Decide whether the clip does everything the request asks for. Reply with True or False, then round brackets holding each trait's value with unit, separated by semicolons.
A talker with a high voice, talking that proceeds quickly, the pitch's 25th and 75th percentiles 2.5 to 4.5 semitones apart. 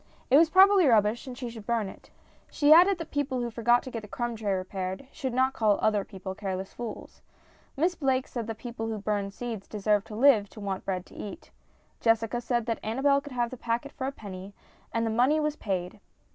True (230 Hz; 220 wpm; 4.2 semitones)